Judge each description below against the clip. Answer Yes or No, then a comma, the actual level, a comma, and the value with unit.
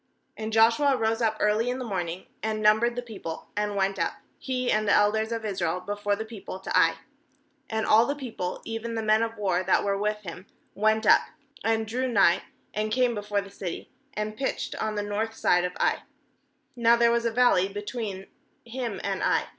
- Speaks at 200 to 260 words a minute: Yes, fast, 205 wpm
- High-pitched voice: Yes, high, 215 Hz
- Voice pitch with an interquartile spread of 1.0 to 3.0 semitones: Yes, narrow, 2.4 semitones